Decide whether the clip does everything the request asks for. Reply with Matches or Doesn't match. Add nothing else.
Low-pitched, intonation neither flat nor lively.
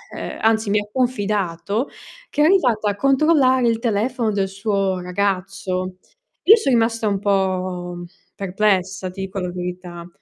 Doesn't match